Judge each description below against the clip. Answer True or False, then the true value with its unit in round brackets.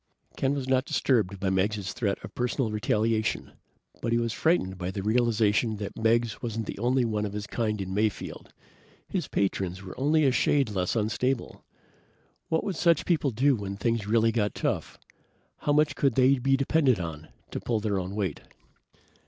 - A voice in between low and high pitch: False (110 Hz)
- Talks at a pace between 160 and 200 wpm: True (180 wpm)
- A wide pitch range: False (4.3 semitones)